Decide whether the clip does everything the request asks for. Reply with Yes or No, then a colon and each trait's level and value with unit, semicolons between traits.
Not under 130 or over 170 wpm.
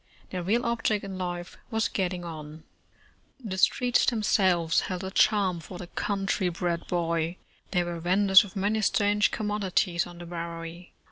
Yes: average, 160 wpm